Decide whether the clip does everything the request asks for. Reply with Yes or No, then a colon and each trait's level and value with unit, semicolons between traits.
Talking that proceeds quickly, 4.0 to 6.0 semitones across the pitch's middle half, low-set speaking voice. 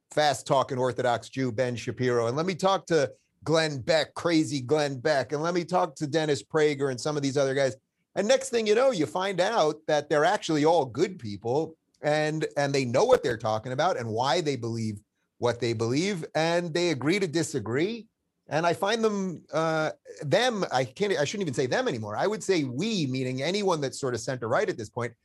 No: fast, 215 wpm; average, 5.2 semitones; medium, 150 Hz